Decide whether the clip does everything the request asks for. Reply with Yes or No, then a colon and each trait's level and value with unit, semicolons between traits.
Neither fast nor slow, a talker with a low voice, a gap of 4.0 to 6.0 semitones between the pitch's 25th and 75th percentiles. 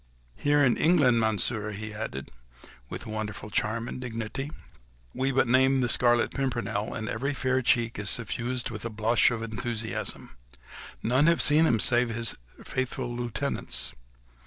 No: average, 150 wpm; low, 120 Hz; average, 2.9 semitones